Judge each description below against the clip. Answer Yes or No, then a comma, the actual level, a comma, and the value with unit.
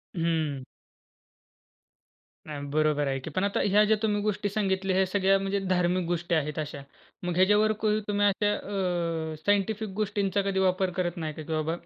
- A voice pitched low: No, medium, 185 Hz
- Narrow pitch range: No, average, 3.8 semitones